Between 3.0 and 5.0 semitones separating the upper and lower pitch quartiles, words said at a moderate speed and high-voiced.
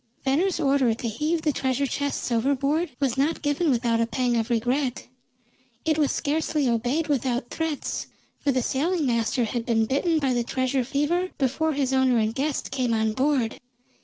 Yes: average, 3.7 semitones; average, 175 wpm; very high, 265 Hz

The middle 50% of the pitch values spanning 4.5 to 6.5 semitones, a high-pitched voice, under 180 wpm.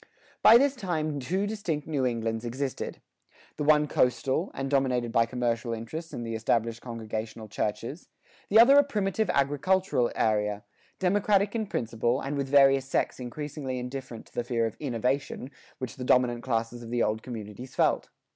No: average, 4.9 semitones; low, 130 Hz; average, 165 wpm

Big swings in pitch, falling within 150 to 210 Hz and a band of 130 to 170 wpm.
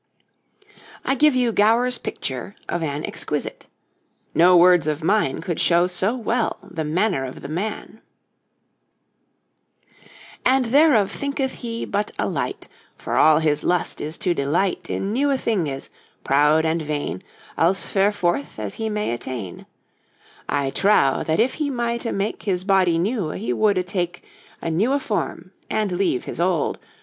Yes: wide, 5.8 semitones; medium, 185 Hz; average, 150 wpm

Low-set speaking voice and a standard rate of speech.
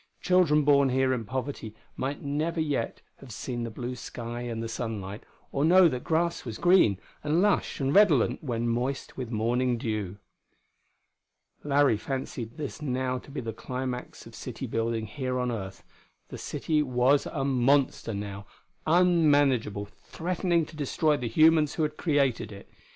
Yes: low, 130 Hz; average, 160 wpm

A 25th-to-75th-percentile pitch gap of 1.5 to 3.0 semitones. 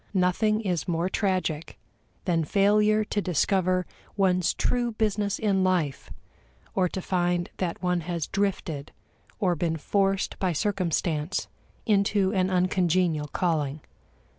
Yes: narrow, 2.6 semitones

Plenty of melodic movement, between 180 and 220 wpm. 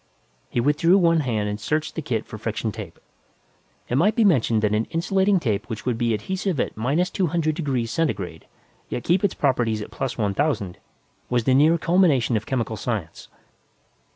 Yes: wide, 7.0 semitones; average, 185 wpm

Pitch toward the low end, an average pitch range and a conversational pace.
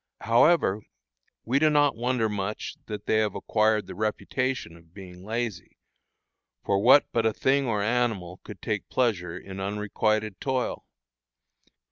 Yes: low, 110 Hz; average, 3.7 semitones; average, 145 wpm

